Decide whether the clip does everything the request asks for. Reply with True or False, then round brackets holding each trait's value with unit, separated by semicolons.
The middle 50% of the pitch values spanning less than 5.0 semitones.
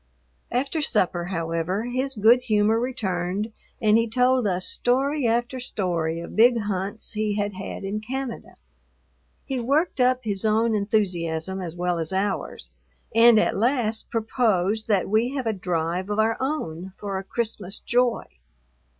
True (4.3 semitones)